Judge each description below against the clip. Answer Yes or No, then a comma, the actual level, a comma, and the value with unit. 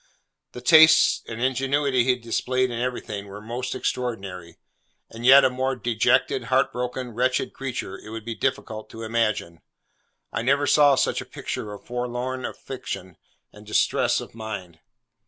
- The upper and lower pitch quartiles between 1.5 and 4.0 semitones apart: Yes, average, 2.9 semitones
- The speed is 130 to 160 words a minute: Yes, average, 155 wpm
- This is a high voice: No, low, 120 Hz